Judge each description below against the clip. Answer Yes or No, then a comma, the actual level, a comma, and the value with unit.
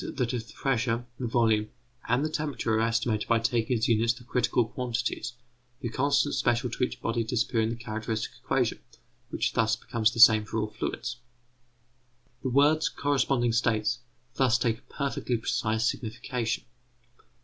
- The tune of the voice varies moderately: No, narrow, 2.0 semitones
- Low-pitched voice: Yes, low, 115 Hz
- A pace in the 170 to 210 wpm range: No, average, 160 wpm